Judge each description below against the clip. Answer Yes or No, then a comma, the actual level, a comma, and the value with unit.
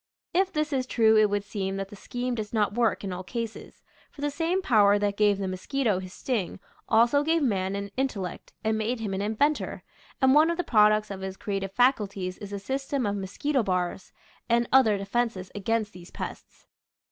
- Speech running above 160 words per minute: Yes, fast, 205 wpm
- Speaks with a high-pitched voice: Yes, high, 215 Hz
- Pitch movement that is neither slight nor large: Yes, average, 4.5 semitones